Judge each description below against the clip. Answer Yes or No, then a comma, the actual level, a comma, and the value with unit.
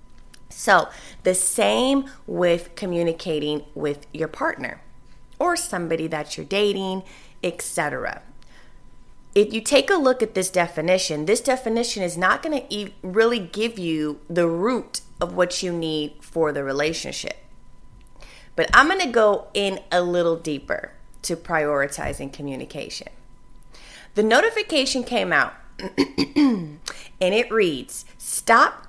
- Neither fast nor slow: No, slow, 125 wpm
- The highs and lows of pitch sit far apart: Yes, wide, 5.7 semitones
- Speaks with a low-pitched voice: No, medium, 180 Hz